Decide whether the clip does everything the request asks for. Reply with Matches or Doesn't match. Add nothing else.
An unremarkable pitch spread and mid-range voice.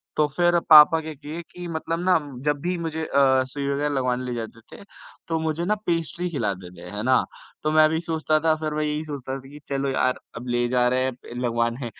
Matches